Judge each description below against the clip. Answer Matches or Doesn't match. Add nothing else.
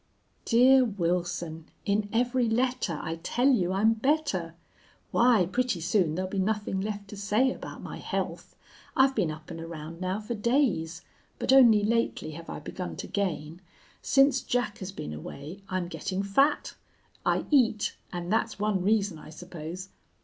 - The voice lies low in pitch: Doesn't match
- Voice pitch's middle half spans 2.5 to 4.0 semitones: Doesn't match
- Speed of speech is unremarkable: Matches